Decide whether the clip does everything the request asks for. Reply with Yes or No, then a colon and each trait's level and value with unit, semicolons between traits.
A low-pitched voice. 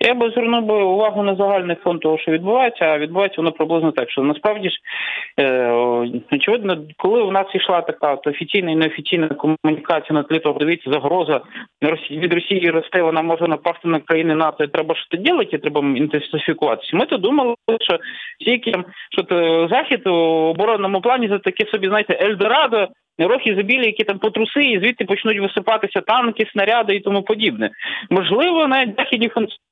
No: high, 190 Hz